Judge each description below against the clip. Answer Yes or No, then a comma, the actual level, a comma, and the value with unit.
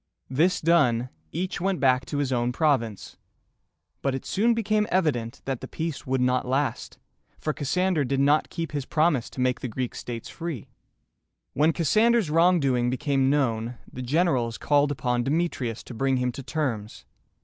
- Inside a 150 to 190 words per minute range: Yes, average, 165 wpm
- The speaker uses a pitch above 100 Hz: Yes, low, 135 Hz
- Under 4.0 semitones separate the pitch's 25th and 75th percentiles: No, average, 4.7 semitones